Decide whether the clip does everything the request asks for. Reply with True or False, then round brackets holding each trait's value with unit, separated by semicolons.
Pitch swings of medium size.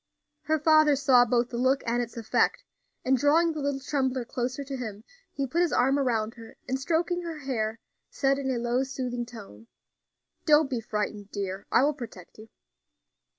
True (3.5 semitones)